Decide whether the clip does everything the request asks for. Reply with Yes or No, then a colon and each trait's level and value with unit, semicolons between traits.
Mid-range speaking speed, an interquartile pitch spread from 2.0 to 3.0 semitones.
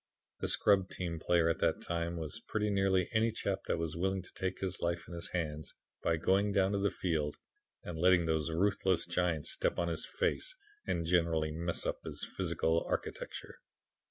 Yes: average, 185 wpm; narrow, 2.6 semitones